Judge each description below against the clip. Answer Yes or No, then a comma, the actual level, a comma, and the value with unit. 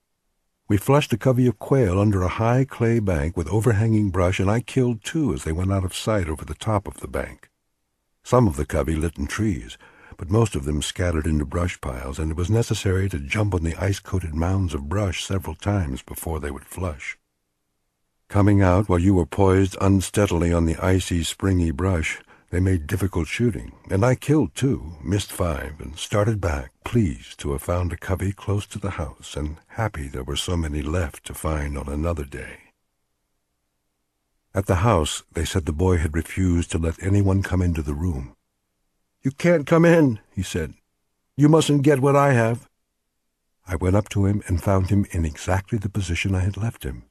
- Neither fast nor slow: Yes, average, 195 wpm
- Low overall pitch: Yes, very low, 90 Hz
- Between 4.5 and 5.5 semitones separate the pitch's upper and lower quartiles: Yes, average, 5.1 semitones